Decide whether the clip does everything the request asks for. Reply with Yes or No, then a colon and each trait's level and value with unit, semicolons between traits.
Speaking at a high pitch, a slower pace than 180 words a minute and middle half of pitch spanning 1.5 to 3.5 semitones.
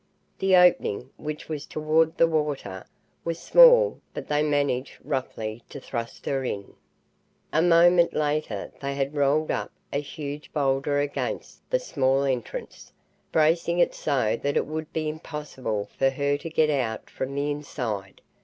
No: medium, 145 Hz; average, 155 wpm; average, 2.8 semitones